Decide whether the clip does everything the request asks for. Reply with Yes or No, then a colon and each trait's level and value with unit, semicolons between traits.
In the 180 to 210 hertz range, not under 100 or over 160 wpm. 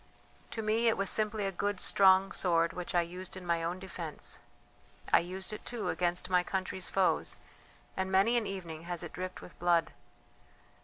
No: medium, 185 Hz; average, 185 wpm